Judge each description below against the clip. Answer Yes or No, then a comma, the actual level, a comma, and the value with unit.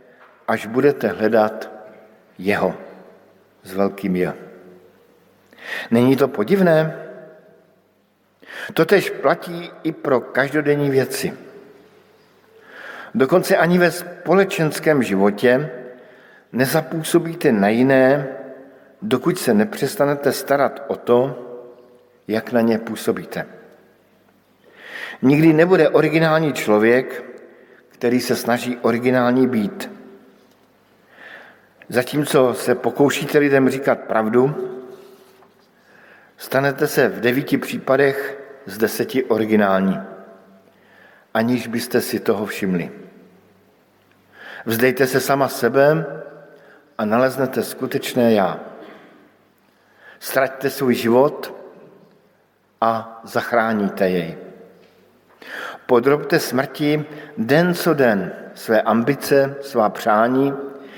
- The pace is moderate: No, slow, 85 wpm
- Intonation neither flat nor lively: Yes, average, 4.6 semitones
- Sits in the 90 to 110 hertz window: No, low, 130 Hz